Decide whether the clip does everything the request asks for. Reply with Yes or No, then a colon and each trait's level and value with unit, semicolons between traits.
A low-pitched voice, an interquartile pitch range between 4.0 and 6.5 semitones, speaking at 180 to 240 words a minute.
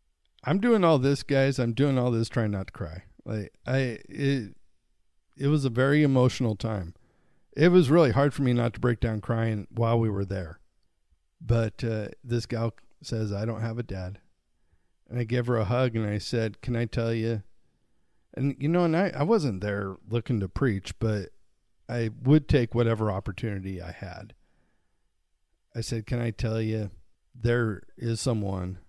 Yes: low, 115 Hz; average, 4.3 semitones; average, 185 wpm